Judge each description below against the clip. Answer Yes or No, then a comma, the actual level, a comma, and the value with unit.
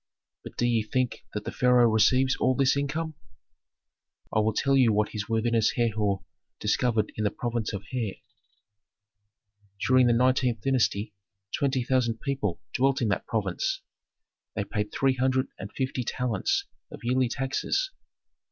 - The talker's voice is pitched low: Yes, low, 120 Hz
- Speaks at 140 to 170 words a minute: Yes, average, 150 wpm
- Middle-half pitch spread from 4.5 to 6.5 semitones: No, average, 3.3 semitones